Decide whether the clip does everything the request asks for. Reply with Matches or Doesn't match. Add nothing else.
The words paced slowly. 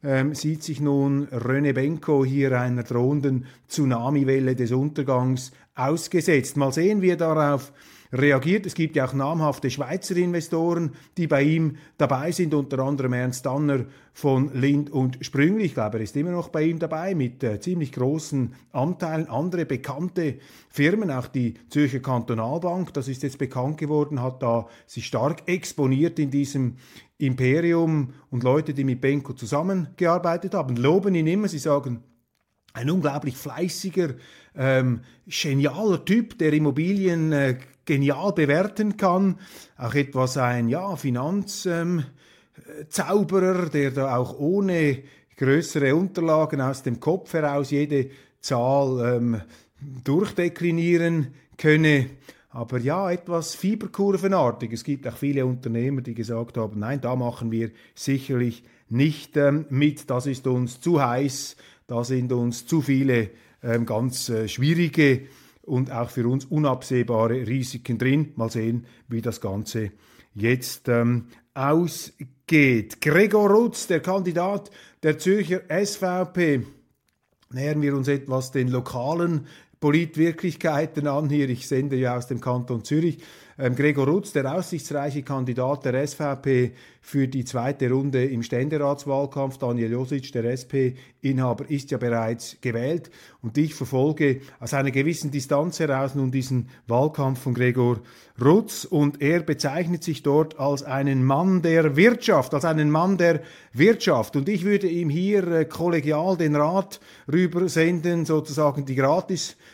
Doesn't match